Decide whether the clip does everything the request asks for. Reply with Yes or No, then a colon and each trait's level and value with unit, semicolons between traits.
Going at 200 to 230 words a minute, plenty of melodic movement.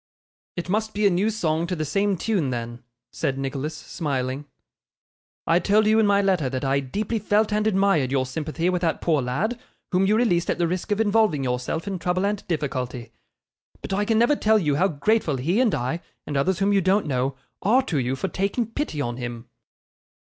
Yes: fast, 205 wpm; wide, 7.0 semitones